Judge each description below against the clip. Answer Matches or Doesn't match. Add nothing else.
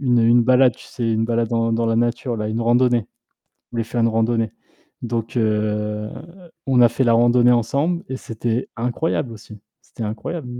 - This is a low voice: Matches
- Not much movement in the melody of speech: Matches